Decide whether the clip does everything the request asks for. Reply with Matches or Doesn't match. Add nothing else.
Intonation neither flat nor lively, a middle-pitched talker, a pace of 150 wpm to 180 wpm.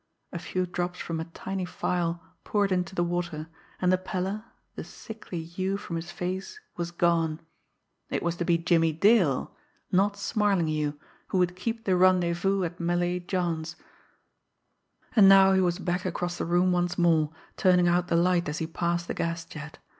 Doesn't match